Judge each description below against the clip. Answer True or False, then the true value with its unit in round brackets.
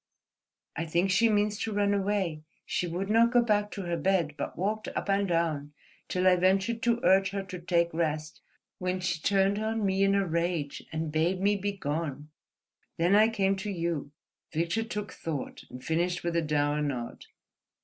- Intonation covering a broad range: False (3.6 semitones)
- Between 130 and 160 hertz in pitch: False (185 Hz)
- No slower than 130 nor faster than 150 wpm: False (190 wpm)